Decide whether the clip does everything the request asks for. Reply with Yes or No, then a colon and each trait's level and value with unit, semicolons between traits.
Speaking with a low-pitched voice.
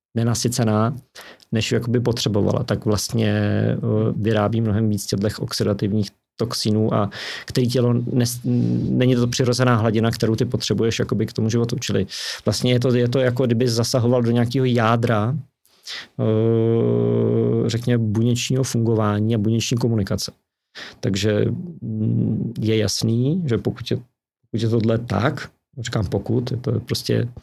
Yes: low, 115 Hz